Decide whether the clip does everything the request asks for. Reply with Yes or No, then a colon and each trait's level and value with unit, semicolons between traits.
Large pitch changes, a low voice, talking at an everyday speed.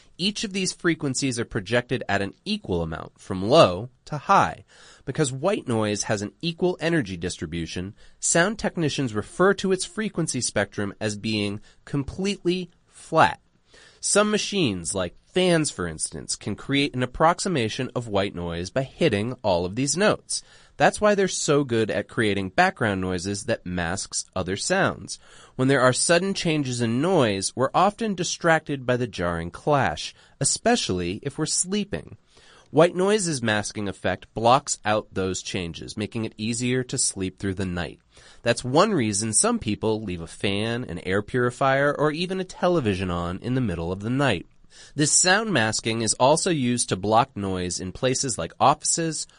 Yes: wide, 8.4 semitones; low, 125 Hz; average, 165 wpm